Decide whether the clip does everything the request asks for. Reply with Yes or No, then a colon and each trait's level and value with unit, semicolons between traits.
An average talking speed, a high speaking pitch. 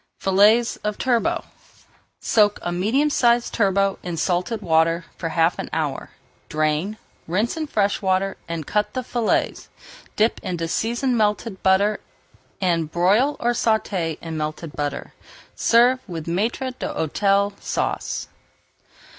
No: slow, 130 wpm; high, 195 Hz